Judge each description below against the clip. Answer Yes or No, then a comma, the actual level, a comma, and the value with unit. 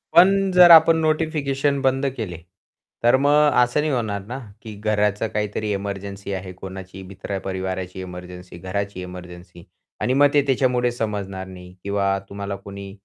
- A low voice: Yes, low, 100 Hz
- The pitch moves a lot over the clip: Yes, wide, 6.0 semitones